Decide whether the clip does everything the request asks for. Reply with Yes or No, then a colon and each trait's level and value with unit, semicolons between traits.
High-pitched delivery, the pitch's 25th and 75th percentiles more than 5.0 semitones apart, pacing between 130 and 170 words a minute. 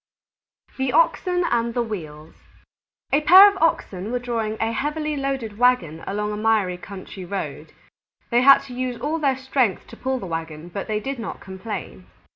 No: high, 230 Hz; wide, 5.5 semitones; average, 180 wpm